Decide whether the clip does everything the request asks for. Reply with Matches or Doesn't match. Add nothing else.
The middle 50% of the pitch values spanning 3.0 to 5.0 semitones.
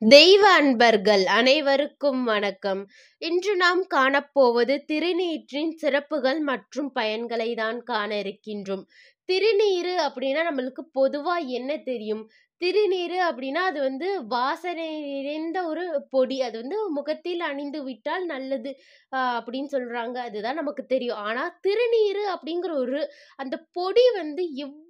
Doesn't match